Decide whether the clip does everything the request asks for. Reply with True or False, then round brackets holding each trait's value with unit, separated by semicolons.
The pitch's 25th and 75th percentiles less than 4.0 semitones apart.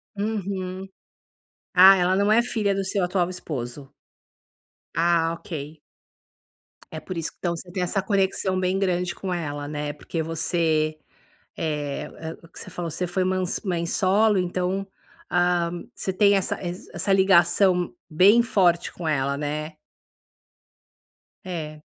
True (2.9 semitones)